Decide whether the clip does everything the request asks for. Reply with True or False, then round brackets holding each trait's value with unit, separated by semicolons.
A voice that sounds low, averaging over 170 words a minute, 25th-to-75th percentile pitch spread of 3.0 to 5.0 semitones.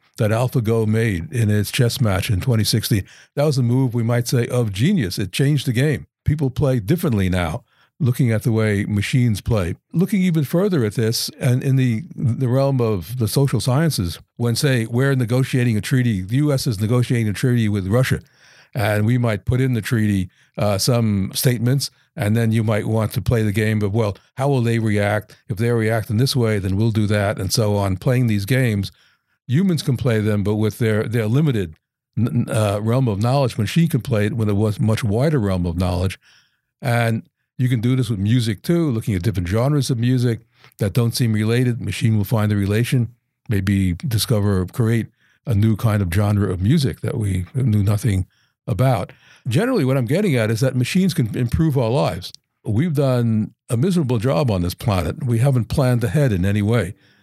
True (115 Hz; 200 wpm; 3.6 semitones)